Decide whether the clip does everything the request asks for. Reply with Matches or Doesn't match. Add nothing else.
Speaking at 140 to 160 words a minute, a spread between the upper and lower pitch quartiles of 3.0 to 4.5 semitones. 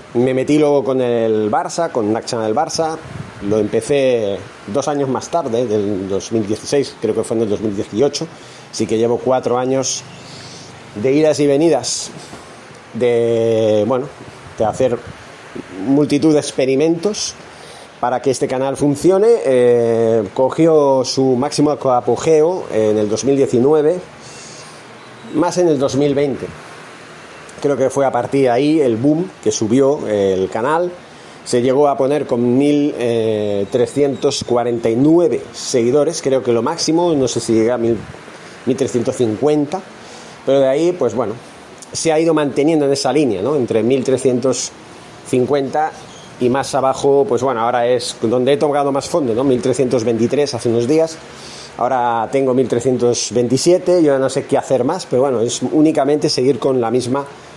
Matches